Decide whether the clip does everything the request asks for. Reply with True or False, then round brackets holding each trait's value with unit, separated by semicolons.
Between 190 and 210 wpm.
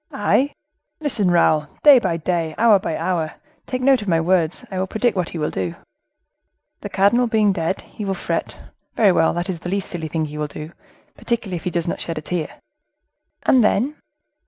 True (195 wpm)